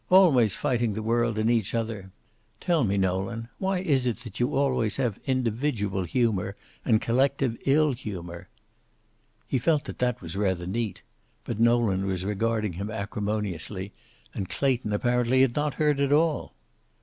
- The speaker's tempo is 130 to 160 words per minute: Yes, average, 155 wpm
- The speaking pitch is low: Yes, low, 115 Hz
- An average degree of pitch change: Yes, average, 4.5 semitones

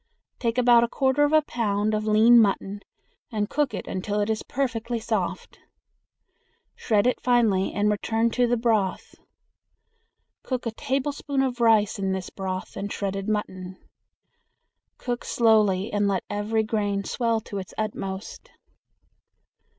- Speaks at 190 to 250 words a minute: No, average, 140 wpm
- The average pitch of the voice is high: Yes, high, 220 Hz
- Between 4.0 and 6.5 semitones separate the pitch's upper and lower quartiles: No, average, 3.0 semitones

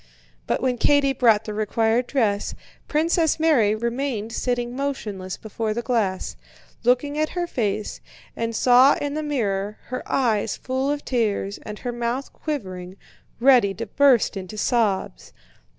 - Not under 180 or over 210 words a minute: No, average, 145 wpm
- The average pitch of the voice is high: Yes, high, 235 Hz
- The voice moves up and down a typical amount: Yes, average, 4.3 semitones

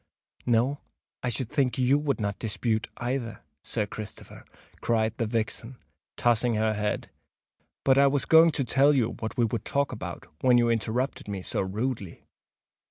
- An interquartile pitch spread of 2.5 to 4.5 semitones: Yes, average, 3.3 semitones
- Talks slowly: No, average, 160 wpm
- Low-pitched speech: Yes, low, 120 Hz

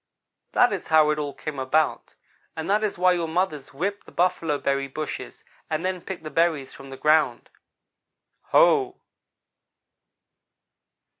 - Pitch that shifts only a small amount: No, average, 3.9 semitones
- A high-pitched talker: No, medium, 160 Hz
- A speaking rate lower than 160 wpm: Yes, average, 145 wpm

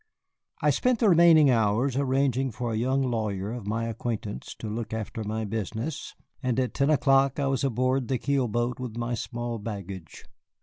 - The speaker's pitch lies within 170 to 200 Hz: No, low, 120 Hz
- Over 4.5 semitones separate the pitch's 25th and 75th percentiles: No, average, 3.4 semitones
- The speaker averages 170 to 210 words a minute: Yes, average, 180 wpm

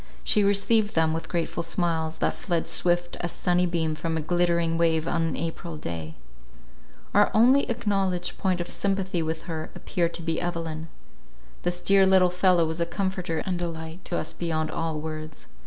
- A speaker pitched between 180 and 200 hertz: No, medium, 170 Hz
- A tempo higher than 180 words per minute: No, average, 175 wpm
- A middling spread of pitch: No, narrow, 2.1 semitones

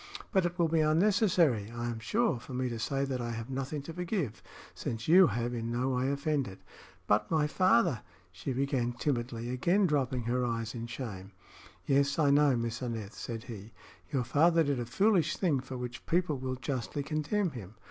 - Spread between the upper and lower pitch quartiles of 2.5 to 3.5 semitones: No, average, 4.7 semitones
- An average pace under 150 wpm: No, average, 195 wpm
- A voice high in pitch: No, low, 130 Hz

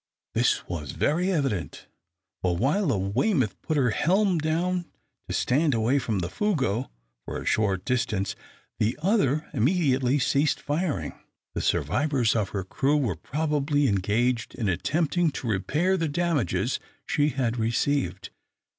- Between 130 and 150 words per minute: Yes, average, 140 wpm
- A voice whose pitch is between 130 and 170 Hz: Yes, low, 135 Hz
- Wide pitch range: Yes, wide, 6.6 semitones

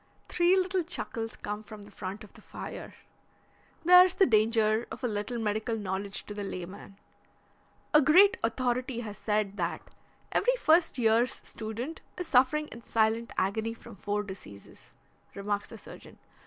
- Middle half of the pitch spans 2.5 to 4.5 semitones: Yes, average, 4.2 semitones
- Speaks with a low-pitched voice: No, high, 225 Hz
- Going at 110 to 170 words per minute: Yes, average, 155 wpm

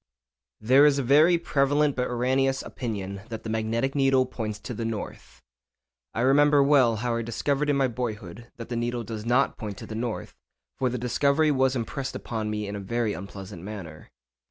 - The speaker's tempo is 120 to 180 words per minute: No, average, 195 wpm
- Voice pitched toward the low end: Yes, low, 120 Hz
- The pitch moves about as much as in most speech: Yes, average, 3.8 semitones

